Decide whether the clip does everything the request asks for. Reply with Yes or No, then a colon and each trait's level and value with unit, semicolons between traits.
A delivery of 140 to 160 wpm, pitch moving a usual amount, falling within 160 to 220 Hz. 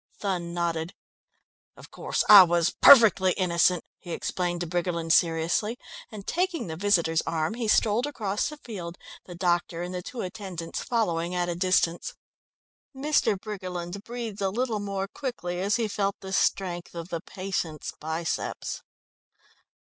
Yes: average, 150 wpm; average, 3.4 semitones; medium, 185 Hz